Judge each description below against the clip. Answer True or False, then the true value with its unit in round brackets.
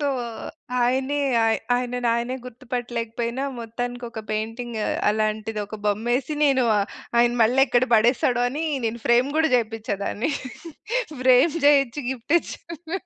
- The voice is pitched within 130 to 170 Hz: False (245 Hz)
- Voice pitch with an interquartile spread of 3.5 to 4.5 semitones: False (2.6 semitones)